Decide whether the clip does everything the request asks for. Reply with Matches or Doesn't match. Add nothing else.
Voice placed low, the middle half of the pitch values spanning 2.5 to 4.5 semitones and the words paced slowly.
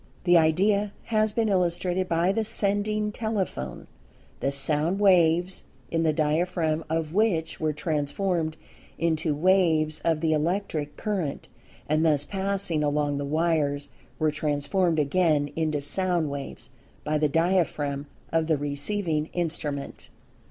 Doesn't match